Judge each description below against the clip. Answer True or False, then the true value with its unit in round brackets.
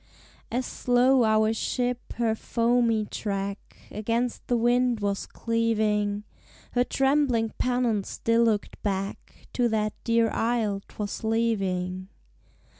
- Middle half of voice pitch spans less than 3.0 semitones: True (2.6 semitones)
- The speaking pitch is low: False (225 Hz)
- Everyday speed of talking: False (115 wpm)